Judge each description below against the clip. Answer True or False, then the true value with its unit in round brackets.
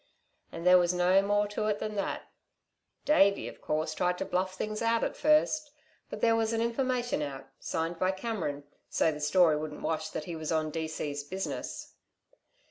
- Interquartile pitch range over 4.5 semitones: True (5.3 semitones)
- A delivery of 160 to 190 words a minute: True (185 wpm)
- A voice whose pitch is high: False (180 Hz)